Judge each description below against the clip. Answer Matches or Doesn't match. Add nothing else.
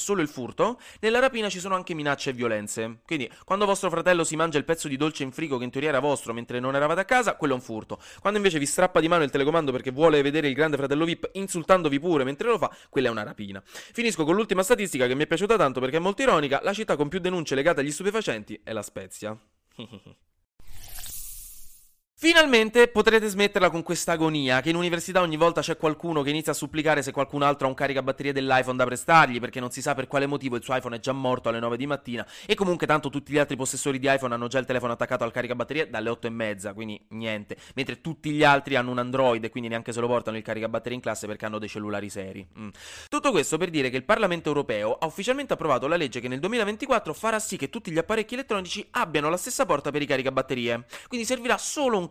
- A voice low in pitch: Doesn't match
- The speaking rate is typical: Doesn't match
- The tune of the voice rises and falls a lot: Matches